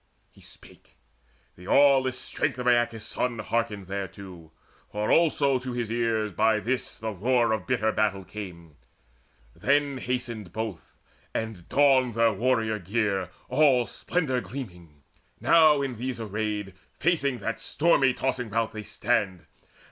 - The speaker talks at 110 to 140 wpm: Yes, slow, 135 wpm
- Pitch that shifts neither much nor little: Yes, average, 3.8 semitones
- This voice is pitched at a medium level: No, low, 115 Hz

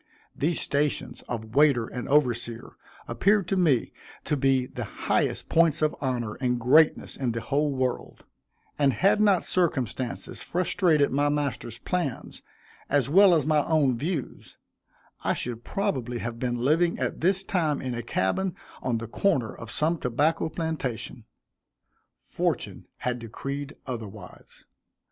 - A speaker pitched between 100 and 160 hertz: Yes, medium, 140 Hz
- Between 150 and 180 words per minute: No, average, 140 wpm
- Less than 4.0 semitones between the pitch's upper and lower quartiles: No, average, 4.9 semitones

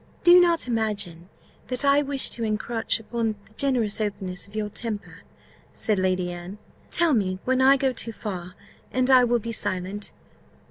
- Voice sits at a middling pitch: No, high, 220 Hz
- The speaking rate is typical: Yes, average, 170 wpm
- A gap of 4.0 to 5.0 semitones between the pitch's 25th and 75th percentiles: Yes, average, 4.3 semitones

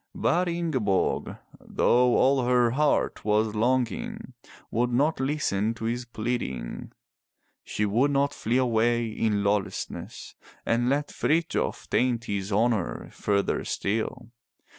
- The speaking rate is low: Yes, slow, 120 wpm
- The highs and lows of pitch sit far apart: No, average, 3.3 semitones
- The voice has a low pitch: Yes, low, 120 Hz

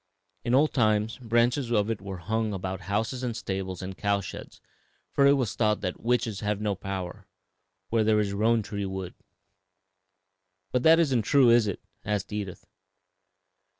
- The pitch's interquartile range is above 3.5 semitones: No, average, 3.2 semitones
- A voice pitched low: Yes, low, 105 Hz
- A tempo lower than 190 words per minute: Yes, average, 165 wpm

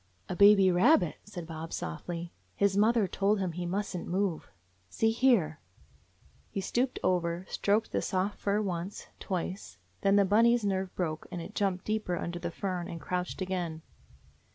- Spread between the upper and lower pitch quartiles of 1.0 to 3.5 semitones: Yes, average, 2.8 semitones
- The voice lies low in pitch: No, medium, 185 Hz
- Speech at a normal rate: Yes, average, 170 wpm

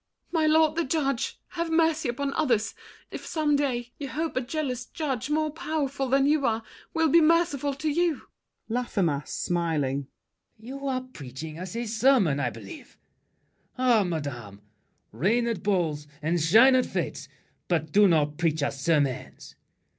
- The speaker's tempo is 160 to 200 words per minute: No, average, 150 wpm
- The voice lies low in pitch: No, high, 245 Hz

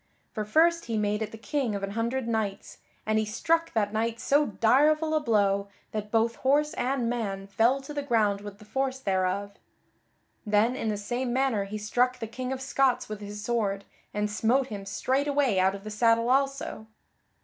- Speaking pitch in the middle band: No, high, 225 Hz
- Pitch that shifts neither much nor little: Yes, average, 4.1 semitones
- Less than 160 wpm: No, average, 195 wpm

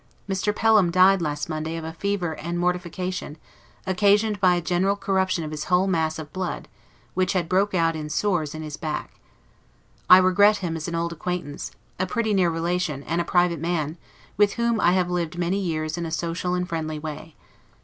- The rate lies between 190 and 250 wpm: Yes, average, 195 wpm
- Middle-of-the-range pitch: Yes, medium, 175 Hz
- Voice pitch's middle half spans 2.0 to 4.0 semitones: Yes, narrow, 2.6 semitones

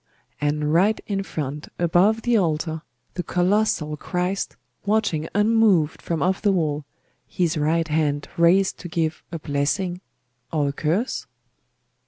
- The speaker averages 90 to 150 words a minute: Yes, slow, 135 wpm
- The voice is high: No, medium, 170 Hz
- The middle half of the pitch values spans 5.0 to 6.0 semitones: No, average, 4.2 semitones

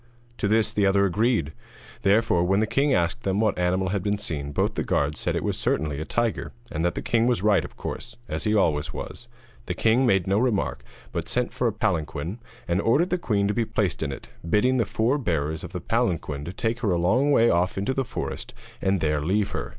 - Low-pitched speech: Yes, low, 100 Hz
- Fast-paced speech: Yes, fast, 235 wpm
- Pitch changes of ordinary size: Yes, average, 4.8 semitones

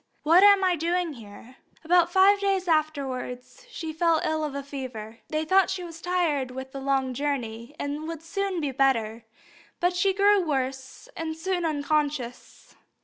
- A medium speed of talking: Yes, average, 170 wpm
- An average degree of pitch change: Yes, average, 5.0 semitones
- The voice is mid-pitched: No, very high, 310 Hz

